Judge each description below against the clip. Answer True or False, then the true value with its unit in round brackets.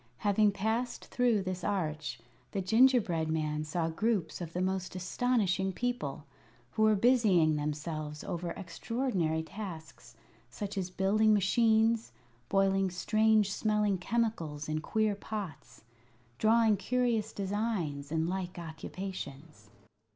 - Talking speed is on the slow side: True (115 wpm)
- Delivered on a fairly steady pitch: False (5.2 semitones)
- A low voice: False (190 Hz)